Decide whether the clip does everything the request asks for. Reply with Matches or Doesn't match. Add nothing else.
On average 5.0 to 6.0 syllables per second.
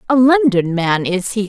Doesn't match